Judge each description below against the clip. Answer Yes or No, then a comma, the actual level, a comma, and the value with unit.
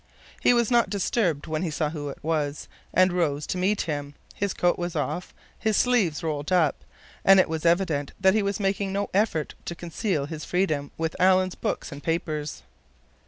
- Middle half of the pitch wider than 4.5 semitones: No, average, 4.1 semitones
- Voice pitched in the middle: Yes, medium, 170 Hz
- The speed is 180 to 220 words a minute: Yes, average, 185 wpm